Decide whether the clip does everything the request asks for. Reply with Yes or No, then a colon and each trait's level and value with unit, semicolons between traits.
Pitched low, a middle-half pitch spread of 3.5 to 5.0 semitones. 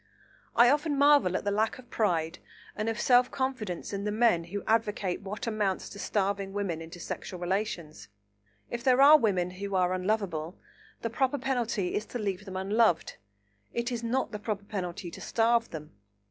No: high, 205 Hz; average, 4.3 semitones